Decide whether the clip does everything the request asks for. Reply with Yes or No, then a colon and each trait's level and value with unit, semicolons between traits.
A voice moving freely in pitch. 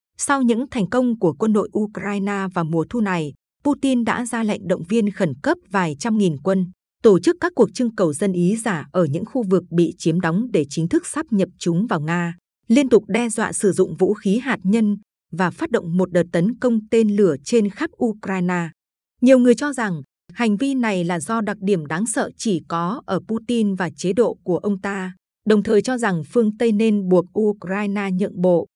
No: average, 4.3 semitones